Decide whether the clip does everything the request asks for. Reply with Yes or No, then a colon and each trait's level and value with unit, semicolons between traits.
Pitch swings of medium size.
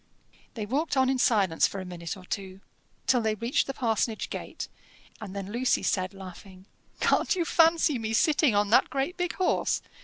No: wide, 5.7 semitones